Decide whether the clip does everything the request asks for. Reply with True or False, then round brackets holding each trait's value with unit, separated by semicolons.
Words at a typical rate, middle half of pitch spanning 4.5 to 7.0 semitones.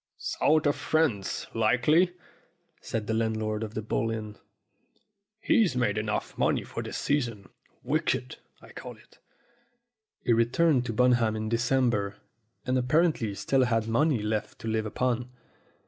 False (145 wpm; 3.0 semitones)